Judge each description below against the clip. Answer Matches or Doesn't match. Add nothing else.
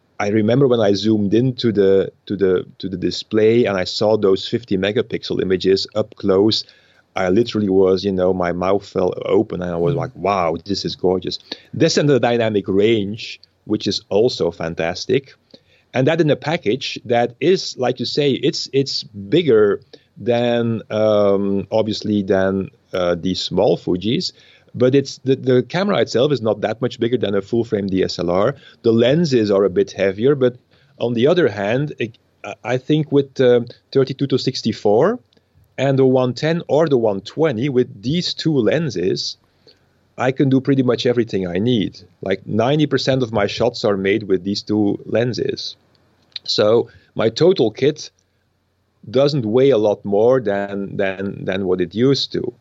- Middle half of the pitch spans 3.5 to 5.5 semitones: Matches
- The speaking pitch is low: Matches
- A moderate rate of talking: Matches